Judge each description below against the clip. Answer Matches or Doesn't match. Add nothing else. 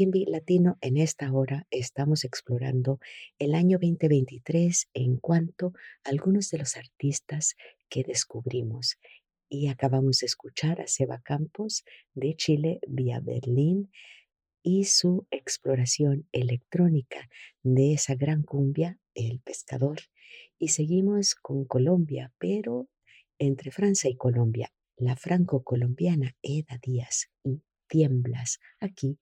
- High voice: Doesn't match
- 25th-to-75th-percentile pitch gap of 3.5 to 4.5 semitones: Doesn't match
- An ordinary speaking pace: Doesn't match